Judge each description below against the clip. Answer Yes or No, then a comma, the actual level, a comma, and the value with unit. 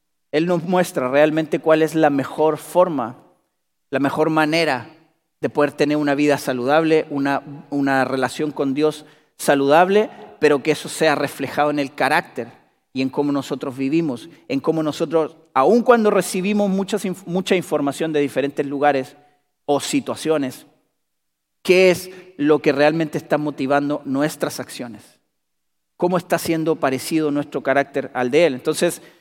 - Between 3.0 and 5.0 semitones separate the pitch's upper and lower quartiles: No, narrow, 2.4 semitones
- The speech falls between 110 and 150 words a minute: Yes, average, 145 wpm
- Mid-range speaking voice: Yes, medium, 150 Hz